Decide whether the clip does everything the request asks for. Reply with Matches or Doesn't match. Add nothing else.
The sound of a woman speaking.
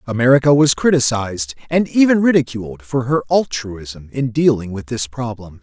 Doesn't match